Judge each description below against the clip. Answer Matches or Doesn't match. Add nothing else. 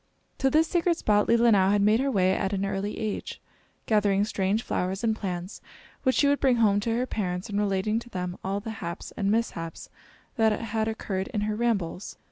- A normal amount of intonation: Matches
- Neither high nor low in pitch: Doesn't match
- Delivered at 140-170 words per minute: Doesn't match